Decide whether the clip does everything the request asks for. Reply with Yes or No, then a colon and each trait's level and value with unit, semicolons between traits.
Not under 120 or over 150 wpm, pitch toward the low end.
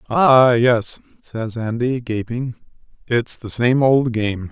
Yes: slow, 135 wpm; low, 120 Hz